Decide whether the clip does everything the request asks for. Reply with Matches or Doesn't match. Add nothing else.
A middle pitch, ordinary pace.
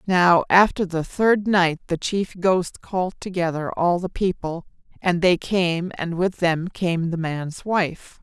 Matches